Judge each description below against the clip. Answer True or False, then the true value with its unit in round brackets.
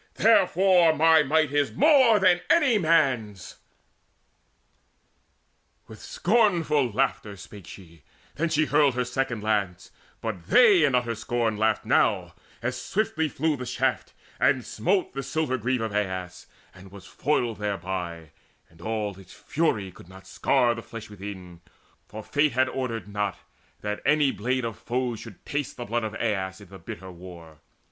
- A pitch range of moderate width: False (7.0 semitones)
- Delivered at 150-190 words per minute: True (155 wpm)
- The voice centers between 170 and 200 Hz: False (120 Hz)